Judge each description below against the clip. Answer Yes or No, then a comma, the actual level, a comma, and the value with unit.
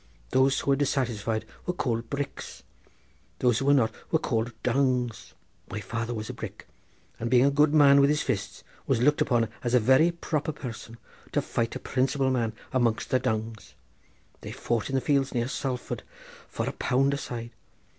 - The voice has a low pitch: Yes, low, 125 Hz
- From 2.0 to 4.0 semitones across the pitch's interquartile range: Yes, average, 3.1 semitones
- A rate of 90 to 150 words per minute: No, average, 185 wpm